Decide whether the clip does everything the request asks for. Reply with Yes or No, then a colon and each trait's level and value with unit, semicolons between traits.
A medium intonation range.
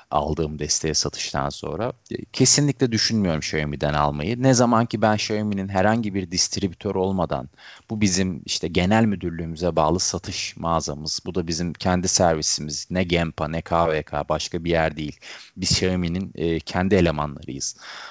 Yes: average, 4.3 semitones